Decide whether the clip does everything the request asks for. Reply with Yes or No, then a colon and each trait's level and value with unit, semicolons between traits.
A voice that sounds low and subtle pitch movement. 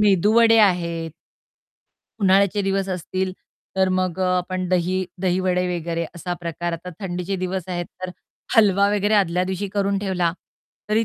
No: medium, 185 Hz; narrow, 2.0 semitones